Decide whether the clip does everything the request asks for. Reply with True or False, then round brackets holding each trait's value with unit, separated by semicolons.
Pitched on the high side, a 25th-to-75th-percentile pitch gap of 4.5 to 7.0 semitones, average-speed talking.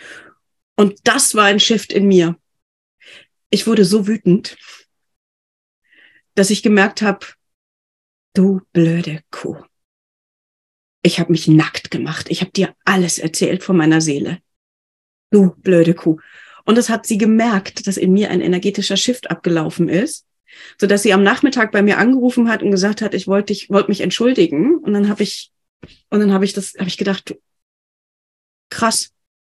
False (195 Hz; 3.4 semitones; 160 wpm)